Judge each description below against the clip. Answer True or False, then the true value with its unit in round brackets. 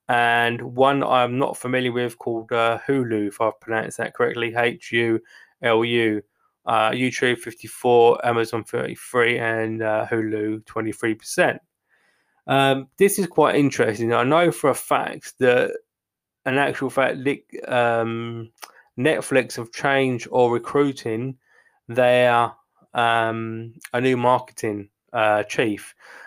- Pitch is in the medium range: False (120 Hz)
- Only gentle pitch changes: True (2.3 semitones)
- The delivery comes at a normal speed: False (120 wpm)